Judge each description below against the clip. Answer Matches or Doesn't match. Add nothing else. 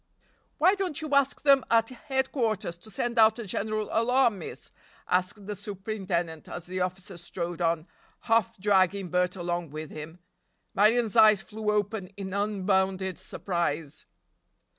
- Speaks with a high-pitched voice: Matches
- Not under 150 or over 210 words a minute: Doesn't match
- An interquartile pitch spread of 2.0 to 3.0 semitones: Doesn't match